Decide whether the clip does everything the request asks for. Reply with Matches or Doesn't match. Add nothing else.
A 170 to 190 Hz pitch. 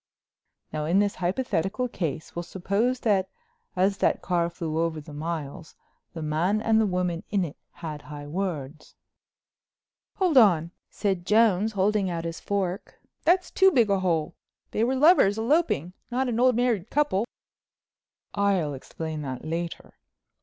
Matches